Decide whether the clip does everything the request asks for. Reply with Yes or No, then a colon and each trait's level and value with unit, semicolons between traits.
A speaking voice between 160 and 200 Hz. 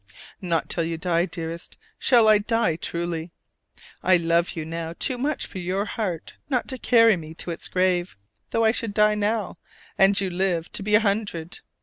Yes: medium, 185 Hz